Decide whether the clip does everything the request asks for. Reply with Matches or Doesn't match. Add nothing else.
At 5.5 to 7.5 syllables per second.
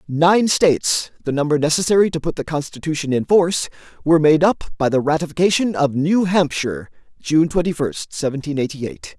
Doesn't match